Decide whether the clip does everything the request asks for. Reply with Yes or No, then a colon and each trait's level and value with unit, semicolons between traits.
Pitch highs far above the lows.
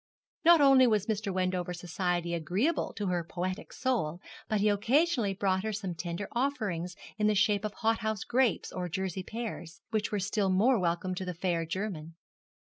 No: average, 3.6 semitones